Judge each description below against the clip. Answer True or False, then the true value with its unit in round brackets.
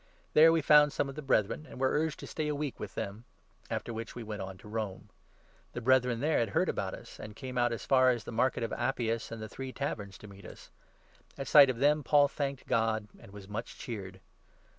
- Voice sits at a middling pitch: False (120 Hz)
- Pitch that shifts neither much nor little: True (4.3 semitones)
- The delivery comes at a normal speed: False (240 wpm)